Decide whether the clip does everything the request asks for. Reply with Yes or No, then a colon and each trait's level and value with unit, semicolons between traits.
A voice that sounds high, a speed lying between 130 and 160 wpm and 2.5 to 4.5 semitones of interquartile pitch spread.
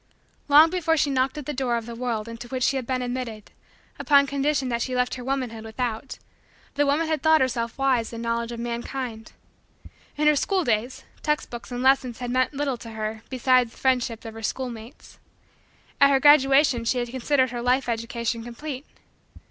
No: very high, 255 Hz; average, 195 wpm; average, 2.8 semitones